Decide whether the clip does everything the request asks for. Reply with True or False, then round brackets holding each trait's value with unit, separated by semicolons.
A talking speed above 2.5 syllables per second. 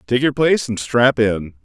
True (4.9 syllables/s)